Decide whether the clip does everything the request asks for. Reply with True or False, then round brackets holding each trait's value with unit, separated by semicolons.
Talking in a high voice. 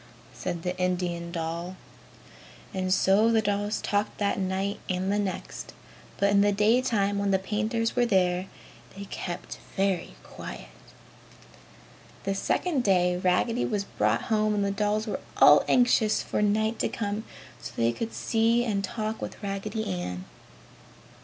True (200 Hz)